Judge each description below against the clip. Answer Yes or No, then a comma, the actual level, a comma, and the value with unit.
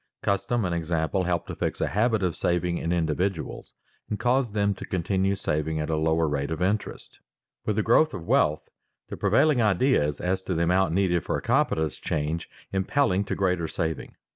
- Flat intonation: No, average, 3.9 semitones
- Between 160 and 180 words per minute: No, average, 190 wpm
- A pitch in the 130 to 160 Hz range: No, very low, 90 Hz